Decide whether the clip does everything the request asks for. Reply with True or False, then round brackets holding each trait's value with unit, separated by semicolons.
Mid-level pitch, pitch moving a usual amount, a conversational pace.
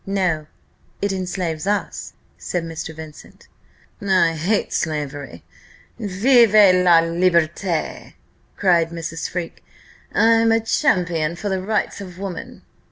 False (180 Hz; 3.5 semitones; 110 wpm)